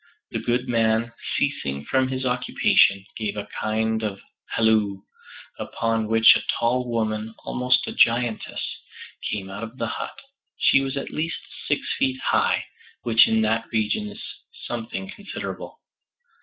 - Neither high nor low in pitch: No, low, 115 Hz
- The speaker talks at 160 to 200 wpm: No, average, 140 wpm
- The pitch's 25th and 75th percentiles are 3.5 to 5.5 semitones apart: No, narrow, 2.5 semitones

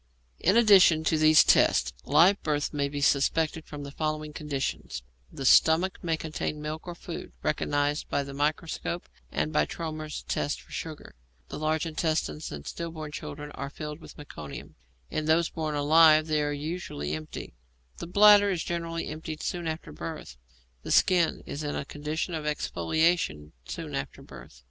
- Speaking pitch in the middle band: Yes, medium, 155 Hz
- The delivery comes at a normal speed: Yes, average, 165 wpm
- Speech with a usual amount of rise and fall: No, narrow, 2.0 semitones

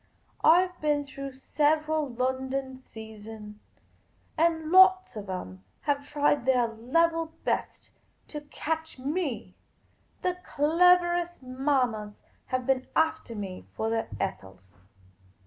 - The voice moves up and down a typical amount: No, wide, 6.1 semitones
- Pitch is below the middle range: No, very high, 275 Hz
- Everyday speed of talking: No, slow, 110 wpm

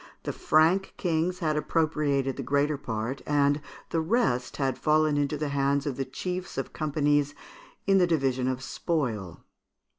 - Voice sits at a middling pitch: Yes, medium, 145 Hz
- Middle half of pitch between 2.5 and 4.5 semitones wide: Yes, average, 2.8 semitones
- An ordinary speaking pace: Yes, average, 155 wpm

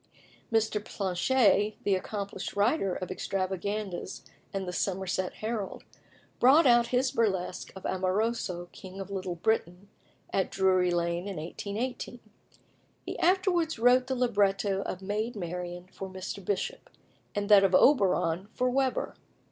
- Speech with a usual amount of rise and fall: Yes, average, 3.7 semitones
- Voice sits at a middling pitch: No, high, 200 Hz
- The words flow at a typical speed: No, slow, 130 wpm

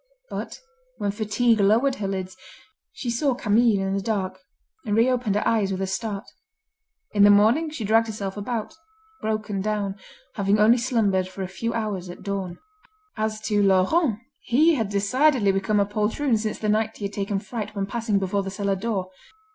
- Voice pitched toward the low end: No, high, 210 Hz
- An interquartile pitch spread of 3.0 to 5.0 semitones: No, narrow, 2.5 semitones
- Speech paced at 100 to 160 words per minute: No, average, 180 wpm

